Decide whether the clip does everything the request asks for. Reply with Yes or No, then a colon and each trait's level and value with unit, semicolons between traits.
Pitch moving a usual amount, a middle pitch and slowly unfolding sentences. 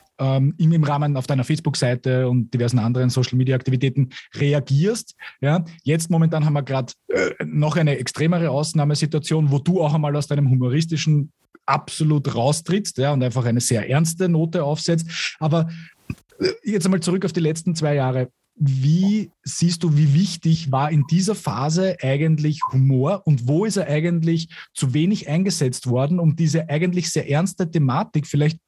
No: average, 3.6 semitones; medium, 150 Hz; average, 155 wpm